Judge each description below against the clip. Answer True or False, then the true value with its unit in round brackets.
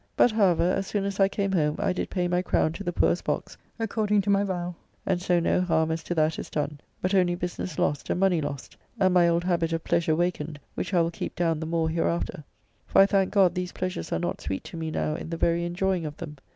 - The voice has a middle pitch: True (175 Hz)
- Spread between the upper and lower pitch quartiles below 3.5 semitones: True (2.6 semitones)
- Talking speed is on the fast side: True (255 wpm)